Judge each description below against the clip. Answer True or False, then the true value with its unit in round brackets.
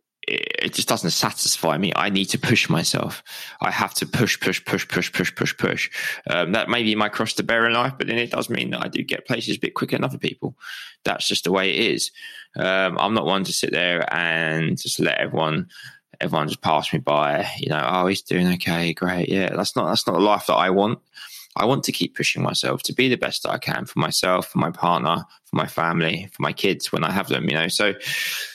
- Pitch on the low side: True (95 Hz)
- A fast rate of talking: True (245 wpm)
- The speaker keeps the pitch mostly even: False (5.0 semitones)